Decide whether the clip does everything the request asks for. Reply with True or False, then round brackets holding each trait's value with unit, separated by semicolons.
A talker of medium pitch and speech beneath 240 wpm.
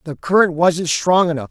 True (170 Hz; 200 wpm)